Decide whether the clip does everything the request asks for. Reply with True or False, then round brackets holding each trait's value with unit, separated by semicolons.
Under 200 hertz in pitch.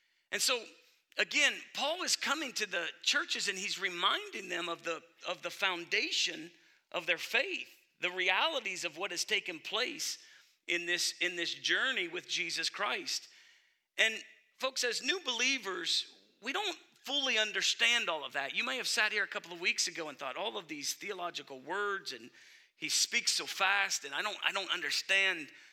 False (210 Hz)